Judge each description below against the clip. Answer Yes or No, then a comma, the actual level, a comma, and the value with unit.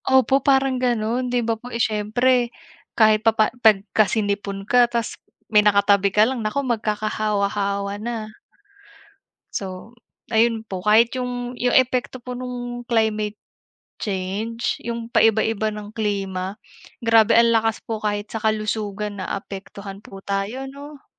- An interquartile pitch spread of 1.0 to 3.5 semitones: Yes, average, 2.8 semitones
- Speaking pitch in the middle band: No, high, 220 Hz